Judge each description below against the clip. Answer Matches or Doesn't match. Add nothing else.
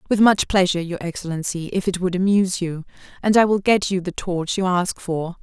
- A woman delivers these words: Matches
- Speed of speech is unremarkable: Doesn't match